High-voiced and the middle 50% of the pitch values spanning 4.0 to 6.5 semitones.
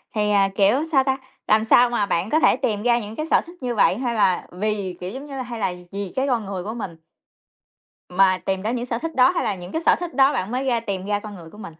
Yes: high, 215 Hz; average, 4.4 semitones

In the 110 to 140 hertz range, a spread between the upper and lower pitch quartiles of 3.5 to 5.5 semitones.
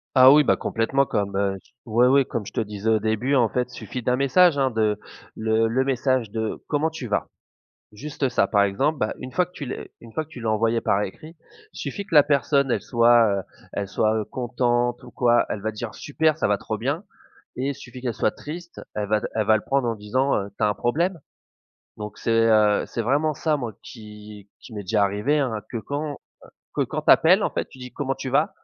Yes: low, 120 Hz; average, 4.2 semitones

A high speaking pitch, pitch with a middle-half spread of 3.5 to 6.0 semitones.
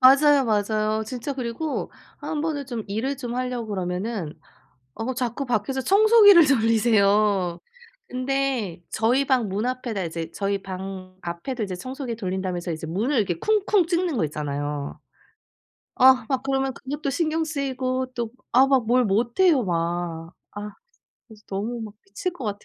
Yes: high, 235 Hz; wide, 5.6 semitones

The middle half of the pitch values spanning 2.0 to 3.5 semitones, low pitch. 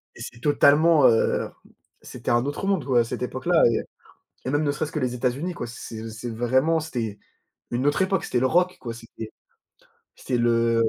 No: average, 4.5 semitones; low, 130 Hz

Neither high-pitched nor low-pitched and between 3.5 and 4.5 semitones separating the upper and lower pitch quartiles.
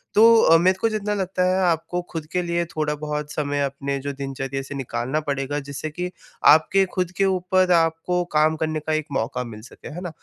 Yes: medium, 155 Hz; average, 4.1 semitones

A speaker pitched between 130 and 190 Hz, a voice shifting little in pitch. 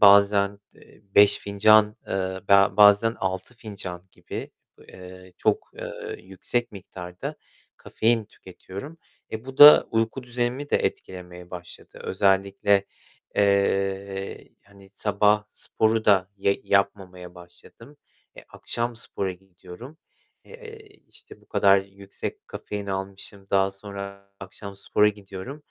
No: low, 100 Hz; narrow, 1.9 semitones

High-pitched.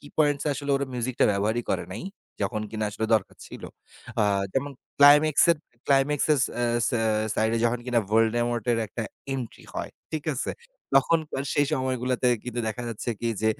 No: low, 125 Hz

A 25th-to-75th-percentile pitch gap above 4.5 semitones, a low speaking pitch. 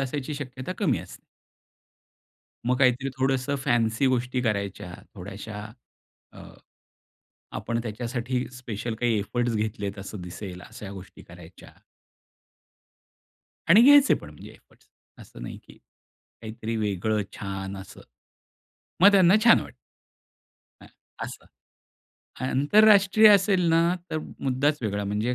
Yes: average, 5.2 semitones; low, 120 Hz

